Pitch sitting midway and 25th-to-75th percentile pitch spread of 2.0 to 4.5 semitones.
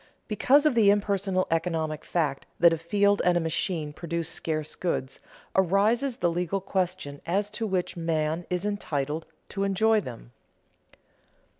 Yes: medium, 180 Hz; average, 3.8 semitones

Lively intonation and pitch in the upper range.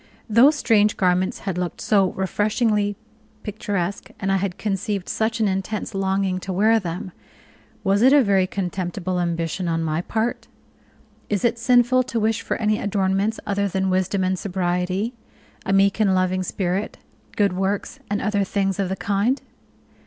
No: narrow, 2.4 semitones; high, 195 Hz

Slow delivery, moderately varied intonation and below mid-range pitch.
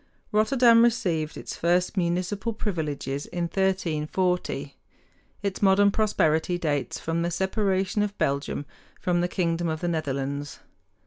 No: slow, 125 wpm; average, 3.8 semitones; medium, 175 Hz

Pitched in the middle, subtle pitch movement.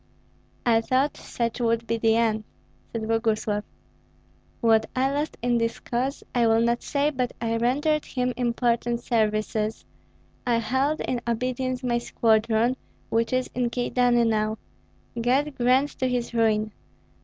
No: high, 235 Hz; narrow, 1.9 semitones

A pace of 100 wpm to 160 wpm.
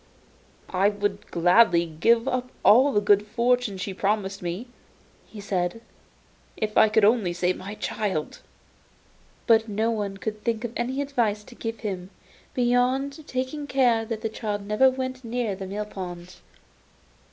Yes: average, 150 wpm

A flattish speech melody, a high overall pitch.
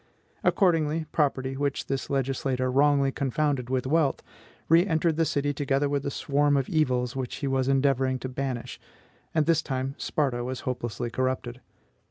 No: narrow, 2.1 semitones; low, 135 Hz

